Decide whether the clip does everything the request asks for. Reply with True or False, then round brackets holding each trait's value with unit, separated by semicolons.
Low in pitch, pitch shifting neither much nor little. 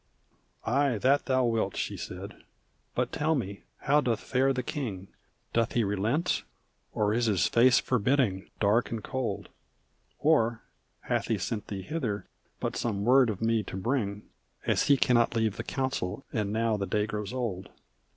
True (115 Hz; 3.9 semitones)